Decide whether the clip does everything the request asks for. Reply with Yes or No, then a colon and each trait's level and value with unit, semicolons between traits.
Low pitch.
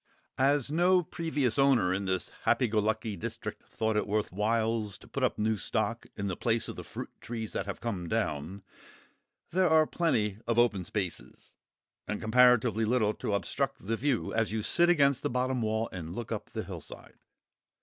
Yes: low, 110 Hz